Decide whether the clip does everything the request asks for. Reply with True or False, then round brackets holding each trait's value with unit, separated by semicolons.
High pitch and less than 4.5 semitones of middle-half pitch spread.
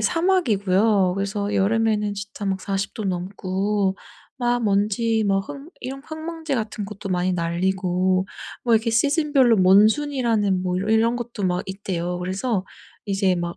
True (205 Hz; 3.7 semitones)